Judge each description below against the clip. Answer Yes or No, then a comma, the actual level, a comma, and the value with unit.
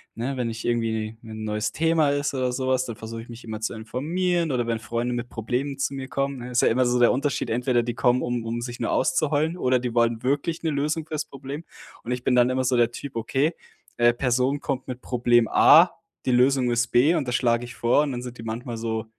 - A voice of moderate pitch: No, low, 125 Hz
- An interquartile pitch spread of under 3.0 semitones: Yes, narrow, 2.6 semitones